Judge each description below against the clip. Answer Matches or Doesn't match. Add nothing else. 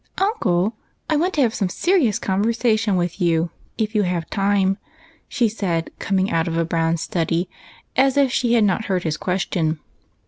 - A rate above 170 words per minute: Matches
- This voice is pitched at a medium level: Doesn't match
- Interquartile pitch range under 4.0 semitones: Doesn't match